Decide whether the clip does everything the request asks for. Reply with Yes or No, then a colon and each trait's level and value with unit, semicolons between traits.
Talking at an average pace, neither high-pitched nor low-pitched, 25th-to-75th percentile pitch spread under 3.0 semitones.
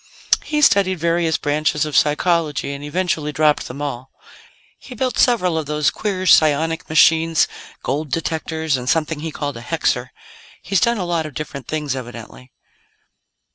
Yes: average, 155 wpm; medium, 155 Hz; narrow, 2.6 semitones